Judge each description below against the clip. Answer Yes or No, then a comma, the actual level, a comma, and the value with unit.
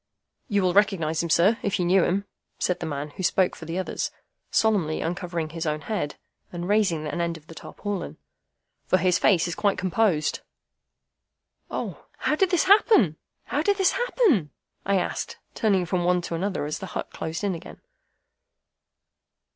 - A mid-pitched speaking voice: Yes, medium, 180 Hz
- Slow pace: No, average, 175 wpm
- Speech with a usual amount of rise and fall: Yes, average, 3.7 semitones